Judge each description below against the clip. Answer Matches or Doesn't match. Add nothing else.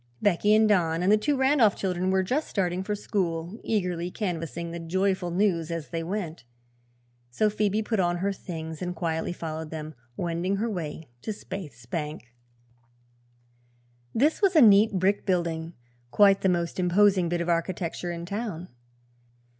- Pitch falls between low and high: Matches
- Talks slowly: Doesn't match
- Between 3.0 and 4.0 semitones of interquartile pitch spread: Matches